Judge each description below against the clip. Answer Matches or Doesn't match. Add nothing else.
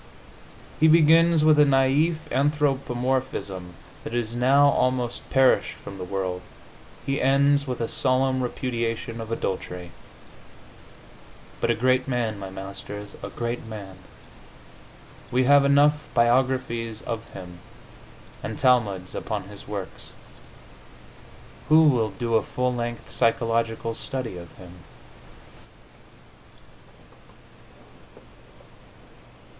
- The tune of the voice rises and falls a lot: Doesn't match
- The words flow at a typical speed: Doesn't match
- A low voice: Matches